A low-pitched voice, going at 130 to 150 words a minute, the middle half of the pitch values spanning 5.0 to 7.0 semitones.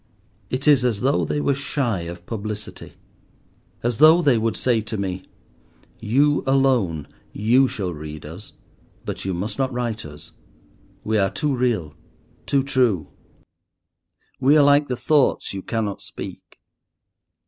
Yes: low, 115 Hz; average, 140 wpm; wide, 5.5 semitones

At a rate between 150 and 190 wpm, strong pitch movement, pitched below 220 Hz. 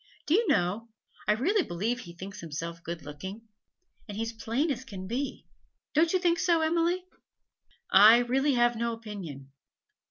No: average, 170 wpm; wide, 7.7 semitones; high, 230 Hz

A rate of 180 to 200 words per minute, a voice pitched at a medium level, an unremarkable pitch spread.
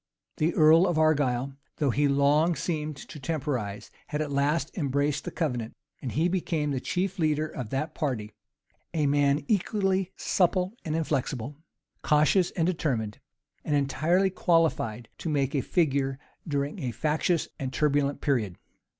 No: average, 150 wpm; medium, 150 Hz; average, 3.2 semitones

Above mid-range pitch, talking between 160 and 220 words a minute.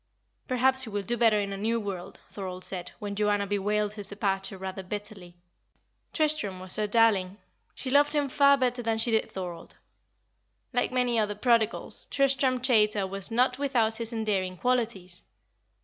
Yes: high, 215 Hz; average, 165 wpm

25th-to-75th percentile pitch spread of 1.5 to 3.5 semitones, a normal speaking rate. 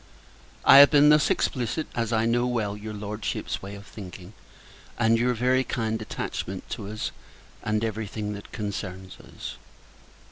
Yes: average, 2.8 semitones; average, 165 wpm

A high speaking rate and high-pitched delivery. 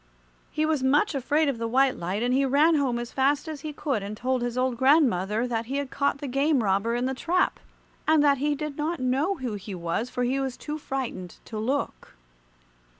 Yes: fast, 220 wpm; very high, 265 Hz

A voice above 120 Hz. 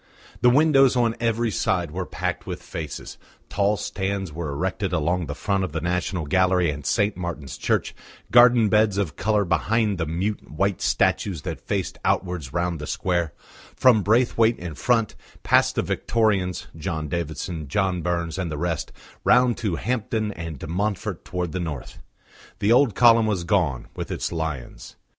No: very low, 90 Hz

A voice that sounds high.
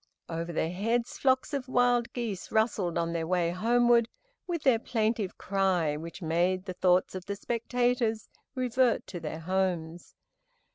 Yes: high, 200 Hz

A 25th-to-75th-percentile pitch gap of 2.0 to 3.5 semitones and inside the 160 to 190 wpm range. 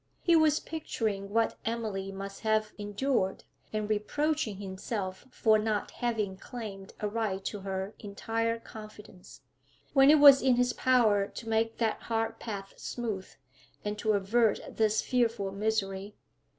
No: average, 2.7 semitones; average, 140 wpm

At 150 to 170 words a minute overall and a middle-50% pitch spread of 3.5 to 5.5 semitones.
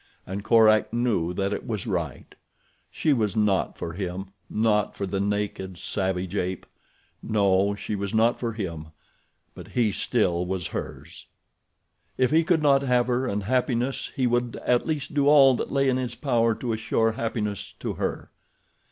Yes: average, 165 wpm; average, 4.2 semitones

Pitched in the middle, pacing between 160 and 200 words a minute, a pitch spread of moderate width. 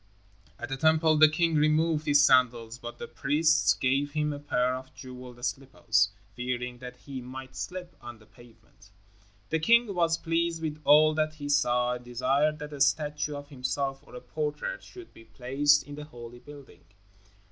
Yes: medium, 145 Hz; average, 180 wpm; average, 3.7 semitones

